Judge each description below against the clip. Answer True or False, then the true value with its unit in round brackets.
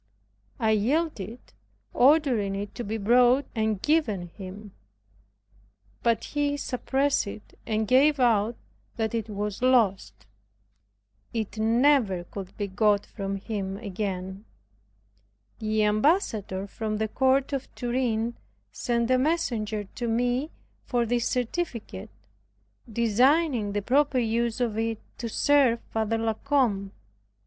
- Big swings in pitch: False (3.6 semitones)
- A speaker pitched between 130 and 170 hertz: False (225 Hz)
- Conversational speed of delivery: False (120 wpm)